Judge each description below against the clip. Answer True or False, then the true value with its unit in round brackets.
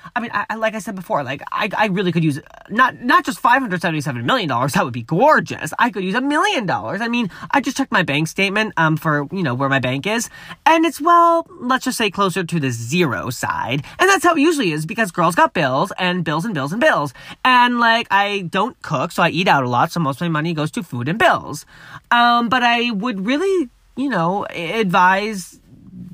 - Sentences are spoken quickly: True (230 wpm)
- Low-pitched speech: False (200 Hz)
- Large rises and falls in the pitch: True (7.1 semitones)